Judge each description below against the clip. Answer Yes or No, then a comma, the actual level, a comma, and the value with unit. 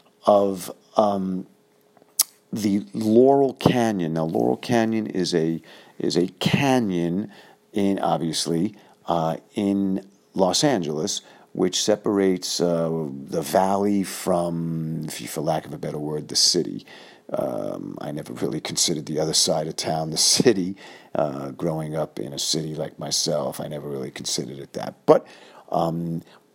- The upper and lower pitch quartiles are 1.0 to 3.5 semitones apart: No, average, 4.3 semitones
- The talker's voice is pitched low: Yes, very low, 85 Hz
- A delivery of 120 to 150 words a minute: Yes, average, 140 wpm